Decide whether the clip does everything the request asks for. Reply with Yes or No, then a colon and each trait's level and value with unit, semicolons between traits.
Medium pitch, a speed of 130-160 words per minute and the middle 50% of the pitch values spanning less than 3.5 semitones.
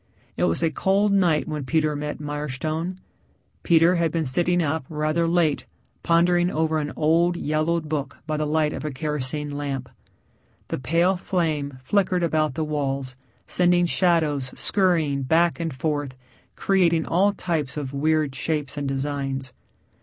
Yes: medium, 155 Hz; average, 150 wpm; average, 2.8 semitones